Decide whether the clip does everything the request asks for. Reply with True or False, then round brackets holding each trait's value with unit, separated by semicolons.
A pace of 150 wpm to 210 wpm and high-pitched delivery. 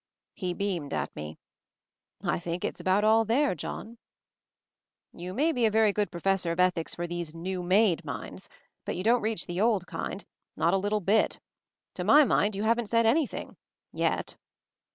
True (185 wpm; 195 Hz)